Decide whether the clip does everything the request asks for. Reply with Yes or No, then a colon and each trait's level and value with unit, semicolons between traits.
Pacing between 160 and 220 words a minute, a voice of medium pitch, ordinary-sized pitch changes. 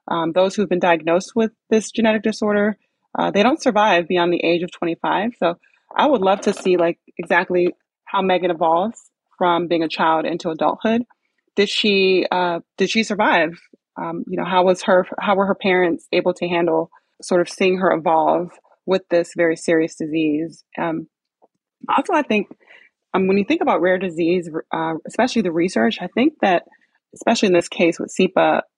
Yes: average, 185 wpm; medium, 180 Hz; average, 3.5 semitones